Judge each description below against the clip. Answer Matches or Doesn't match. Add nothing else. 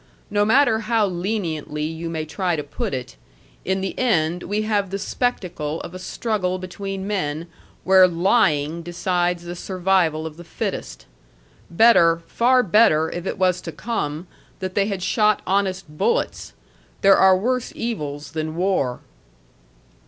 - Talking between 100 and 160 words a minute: Matches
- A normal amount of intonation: Matches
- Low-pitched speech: Doesn't match